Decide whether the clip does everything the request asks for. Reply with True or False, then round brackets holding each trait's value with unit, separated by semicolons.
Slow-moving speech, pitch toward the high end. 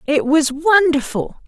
True (120 wpm; 305 Hz)